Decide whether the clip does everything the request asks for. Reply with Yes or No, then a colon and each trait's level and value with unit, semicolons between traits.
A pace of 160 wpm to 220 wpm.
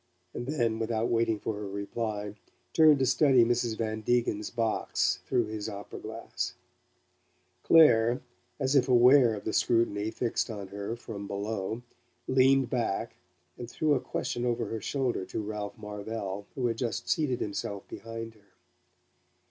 No: average, 150 wpm